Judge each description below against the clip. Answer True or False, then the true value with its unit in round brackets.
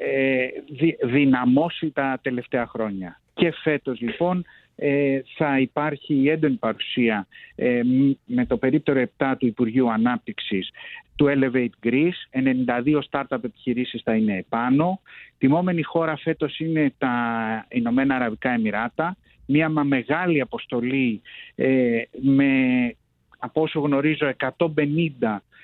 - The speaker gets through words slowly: True (110 wpm)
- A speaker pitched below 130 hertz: False (135 Hz)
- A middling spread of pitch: True (4.0 semitones)